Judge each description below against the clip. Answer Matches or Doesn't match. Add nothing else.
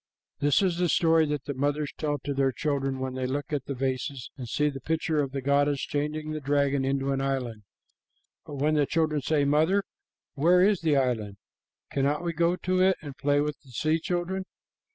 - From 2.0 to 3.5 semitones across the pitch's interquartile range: Matches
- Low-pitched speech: Doesn't match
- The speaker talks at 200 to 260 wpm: Matches